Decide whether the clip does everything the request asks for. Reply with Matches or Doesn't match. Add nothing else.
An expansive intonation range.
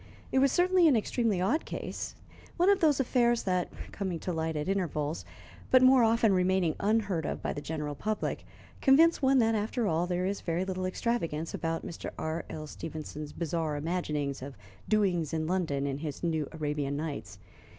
Matches